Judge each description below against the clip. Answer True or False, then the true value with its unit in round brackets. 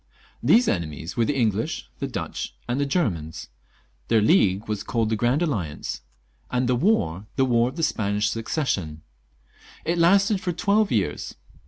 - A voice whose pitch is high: False (115 Hz)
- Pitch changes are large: True (7.9 semitones)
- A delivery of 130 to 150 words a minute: False (165 wpm)